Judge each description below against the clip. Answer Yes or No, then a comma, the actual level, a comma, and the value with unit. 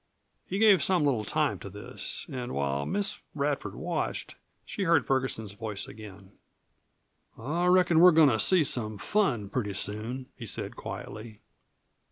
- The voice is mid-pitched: No, low, 125 Hz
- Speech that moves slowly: No, average, 150 wpm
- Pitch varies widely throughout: Yes, wide, 8.4 semitones